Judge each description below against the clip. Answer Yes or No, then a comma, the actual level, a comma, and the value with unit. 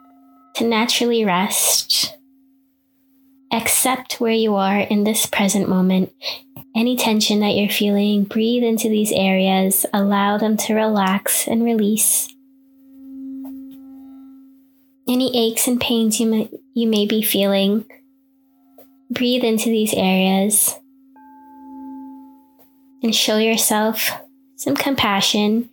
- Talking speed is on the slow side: Yes, slow, 105 wpm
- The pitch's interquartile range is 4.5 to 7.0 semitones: No, average, 4.0 semitones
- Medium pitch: No, high, 235 Hz